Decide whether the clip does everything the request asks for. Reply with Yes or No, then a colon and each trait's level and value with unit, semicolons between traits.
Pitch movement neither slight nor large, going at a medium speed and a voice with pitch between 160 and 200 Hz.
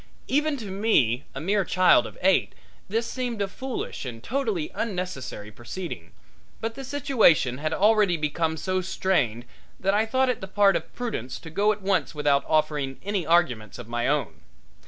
No: wide, 6.7 semitones; average, 175 wpm; medium, 185 Hz